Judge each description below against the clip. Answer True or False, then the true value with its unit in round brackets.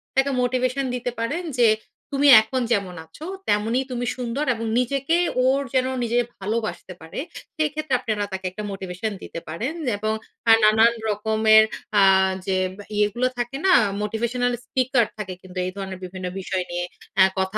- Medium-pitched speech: False (225 Hz)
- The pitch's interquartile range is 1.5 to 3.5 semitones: False (4.1 semitones)